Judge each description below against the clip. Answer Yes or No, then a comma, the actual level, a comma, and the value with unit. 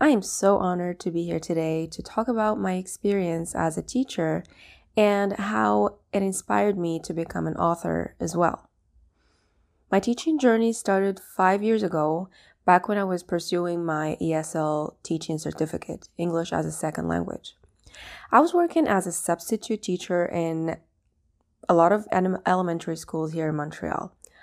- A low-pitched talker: No, medium, 175 Hz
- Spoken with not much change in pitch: No, average, 3.9 semitones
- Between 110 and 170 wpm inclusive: Yes, average, 155 wpm